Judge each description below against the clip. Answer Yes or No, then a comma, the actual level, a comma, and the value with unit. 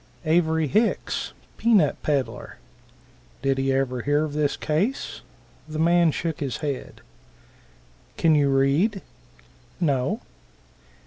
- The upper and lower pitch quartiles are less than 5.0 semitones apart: Yes, average, 3.8 semitones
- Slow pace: Yes, slow, 115 wpm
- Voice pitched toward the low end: No, medium, 150 Hz